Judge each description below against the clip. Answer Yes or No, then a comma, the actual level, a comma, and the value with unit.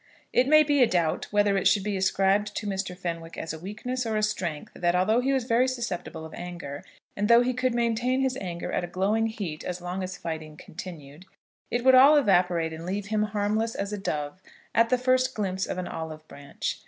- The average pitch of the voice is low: No, high, 200 Hz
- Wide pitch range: No, average, 5.0 semitones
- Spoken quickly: Yes, fast, 215 wpm